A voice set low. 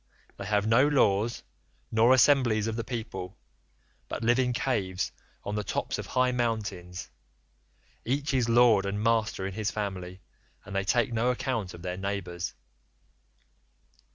Yes: low, 110 Hz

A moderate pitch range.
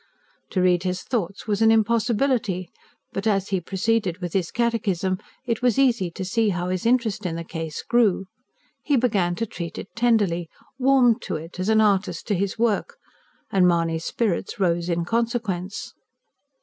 Yes: average, 4.4 semitones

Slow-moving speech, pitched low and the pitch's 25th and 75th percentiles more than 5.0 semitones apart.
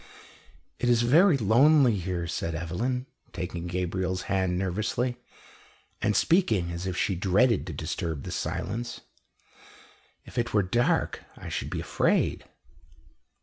Yes: slow, 130 wpm; very low, 95 Hz; wide, 5.4 semitones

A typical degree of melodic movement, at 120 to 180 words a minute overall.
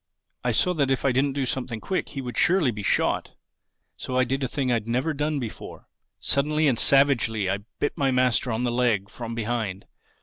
No: average, 3.2 semitones; fast, 205 wpm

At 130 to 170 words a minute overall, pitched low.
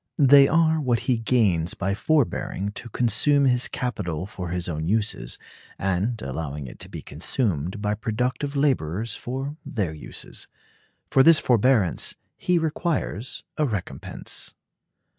Yes: slow, 135 wpm; low, 115 Hz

